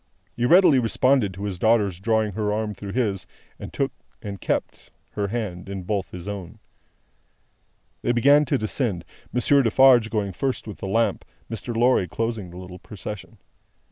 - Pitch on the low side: Yes, low, 110 Hz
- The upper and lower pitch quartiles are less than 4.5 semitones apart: Yes, average, 3.8 semitones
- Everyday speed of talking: Yes, average, 165 wpm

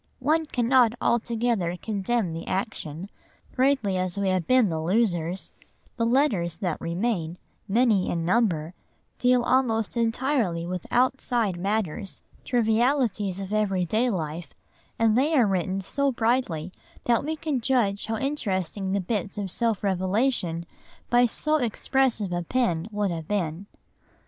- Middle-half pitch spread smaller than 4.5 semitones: No, average, 5.0 semitones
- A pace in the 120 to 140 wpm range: Yes, slow, 135 wpm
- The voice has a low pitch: No, high, 210 Hz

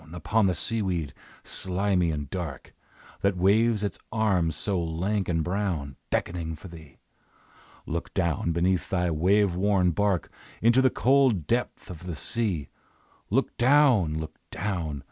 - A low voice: Yes, very low, 90 Hz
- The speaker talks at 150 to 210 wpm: No, average, 140 wpm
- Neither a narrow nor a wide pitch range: Yes, average, 3.9 semitones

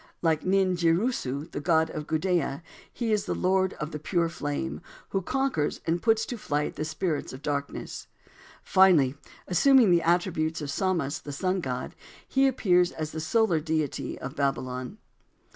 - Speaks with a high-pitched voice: No, medium, 165 Hz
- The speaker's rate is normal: Yes, average, 160 wpm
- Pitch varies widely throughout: No, average, 4.1 semitones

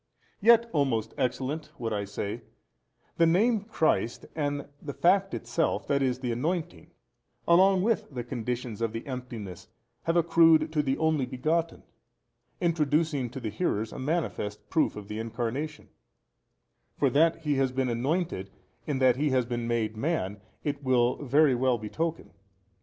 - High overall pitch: No, low, 135 Hz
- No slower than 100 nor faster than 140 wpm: No, average, 155 wpm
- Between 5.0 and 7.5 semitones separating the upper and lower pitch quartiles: Yes, wide, 5.4 semitones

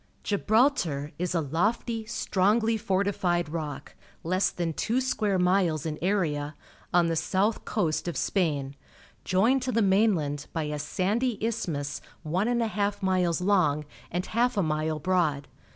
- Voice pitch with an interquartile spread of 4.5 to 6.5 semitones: Yes, average, 5.2 semitones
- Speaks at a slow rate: No, average, 150 wpm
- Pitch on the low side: No, medium, 185 Hz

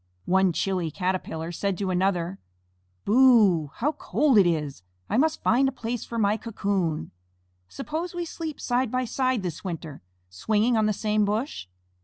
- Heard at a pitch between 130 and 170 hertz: No, high, 210 Hz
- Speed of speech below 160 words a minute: No, average, 165 wpm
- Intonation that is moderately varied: No, wide, 5.9 semitones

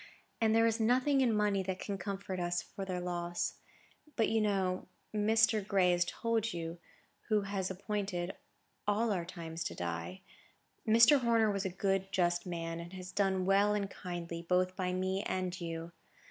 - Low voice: No, high, 190 Hz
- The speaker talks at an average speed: Yes, average, 165 wpm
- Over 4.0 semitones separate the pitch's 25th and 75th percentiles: No, average, 3.0 semitones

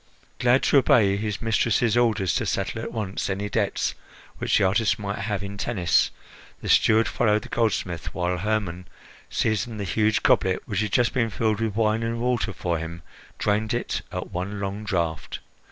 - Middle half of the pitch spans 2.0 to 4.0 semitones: Yes, average, 2.8 semitones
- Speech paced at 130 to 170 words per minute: No, average, 180 wpm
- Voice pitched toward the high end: No, low, 105 Hz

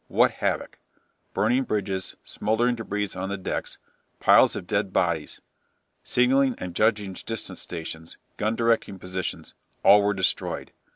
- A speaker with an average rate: No, slow, 130 wpm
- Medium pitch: No, low, 105 Hz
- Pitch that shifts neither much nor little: Yes, average, 3.5 semitones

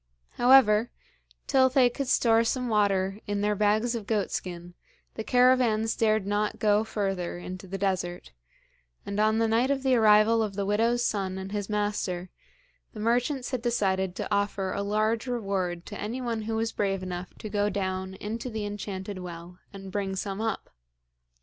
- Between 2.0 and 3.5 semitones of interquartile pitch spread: Yes, average, 2.8 semitones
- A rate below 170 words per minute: No, average, 175 wpm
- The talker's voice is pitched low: No, high, 210 Hz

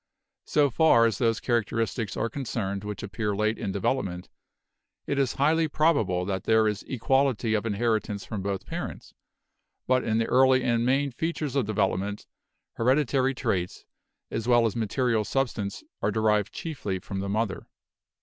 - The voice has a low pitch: Yes, low, 115 Hz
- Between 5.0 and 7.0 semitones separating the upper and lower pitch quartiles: No, average, 4.2 semitones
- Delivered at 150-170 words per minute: Yes, average, 155 wpm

